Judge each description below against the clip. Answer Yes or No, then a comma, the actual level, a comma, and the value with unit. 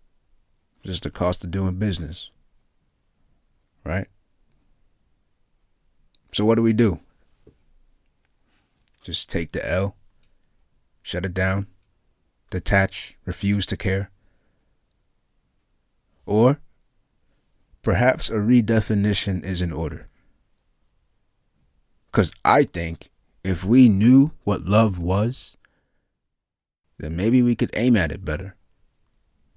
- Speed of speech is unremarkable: No, slow, 95 wpm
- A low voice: Yes, very low, 95 Hz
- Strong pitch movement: No, average, 3.8 semitones